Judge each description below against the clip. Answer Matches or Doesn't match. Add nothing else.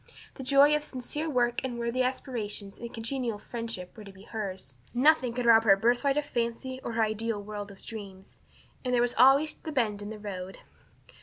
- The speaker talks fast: Matches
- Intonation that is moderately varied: Matches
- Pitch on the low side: Doesn't match